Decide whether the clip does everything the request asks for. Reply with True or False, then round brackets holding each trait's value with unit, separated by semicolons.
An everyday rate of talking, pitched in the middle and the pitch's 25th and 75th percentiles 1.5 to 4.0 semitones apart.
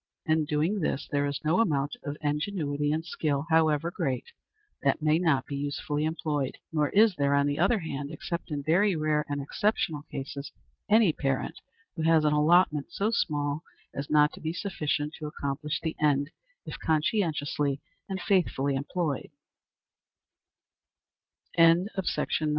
True (150 wpm; 150 Hz; 2.5 semitones)